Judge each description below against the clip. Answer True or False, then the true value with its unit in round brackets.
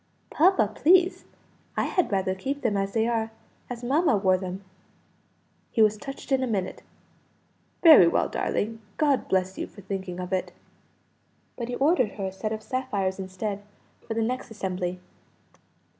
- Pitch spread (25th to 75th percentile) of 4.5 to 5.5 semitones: True (5.2 semitones)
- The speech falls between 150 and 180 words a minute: True (160 wpm)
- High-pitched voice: True (215 Hz)